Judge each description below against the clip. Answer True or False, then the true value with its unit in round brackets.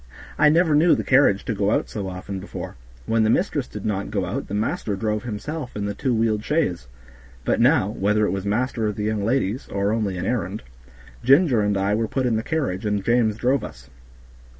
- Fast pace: True (220 wpm)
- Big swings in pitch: False (3.7 semitones)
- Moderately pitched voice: False (110 Hz)